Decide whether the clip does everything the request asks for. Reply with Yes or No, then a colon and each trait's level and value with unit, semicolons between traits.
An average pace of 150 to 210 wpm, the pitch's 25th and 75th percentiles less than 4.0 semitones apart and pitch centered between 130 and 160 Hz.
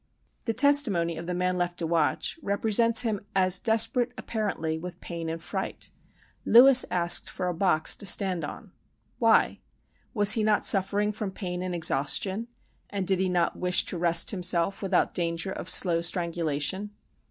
No: average, 165 wpm; average, 3.4 semitones; medium, 185 Hz